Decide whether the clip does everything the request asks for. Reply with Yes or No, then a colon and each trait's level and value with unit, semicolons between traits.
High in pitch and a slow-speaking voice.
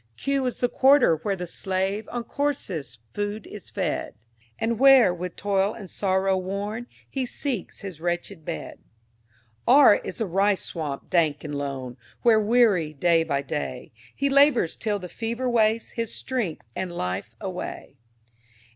No: high, 200 Hz; average, 155 wpm